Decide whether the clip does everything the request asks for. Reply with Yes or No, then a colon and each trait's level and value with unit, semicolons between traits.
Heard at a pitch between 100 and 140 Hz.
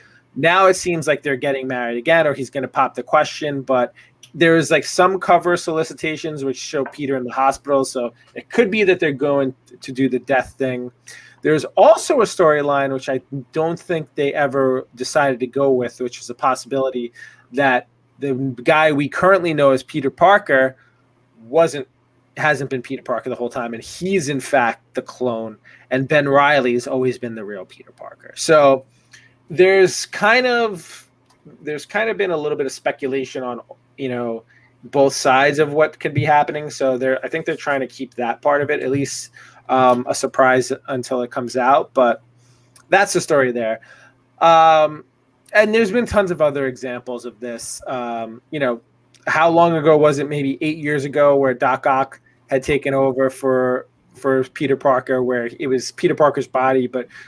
Yes: low, 135 Hz